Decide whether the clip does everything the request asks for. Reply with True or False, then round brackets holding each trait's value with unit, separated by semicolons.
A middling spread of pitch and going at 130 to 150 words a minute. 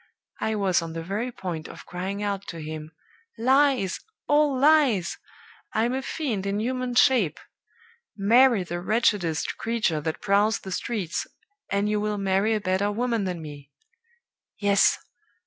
True (4.5 semitones; 145 wpm)